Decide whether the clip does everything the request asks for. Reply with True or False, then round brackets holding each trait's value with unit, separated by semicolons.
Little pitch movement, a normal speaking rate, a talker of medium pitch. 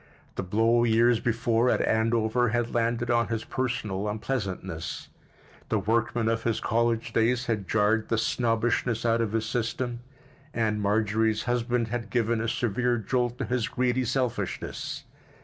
False (1.5 semitones; 150 wpm; 115 Hz)